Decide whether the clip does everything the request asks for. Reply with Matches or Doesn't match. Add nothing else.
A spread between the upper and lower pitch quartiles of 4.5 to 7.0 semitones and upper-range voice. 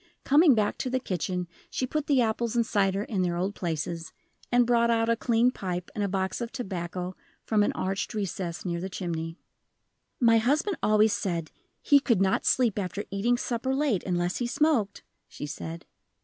Matches